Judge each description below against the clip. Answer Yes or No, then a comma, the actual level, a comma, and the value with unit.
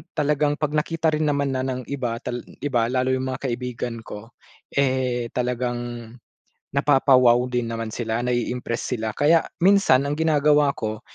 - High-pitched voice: No, low, 130 Hz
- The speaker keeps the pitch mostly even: No, average, 3.2 semitones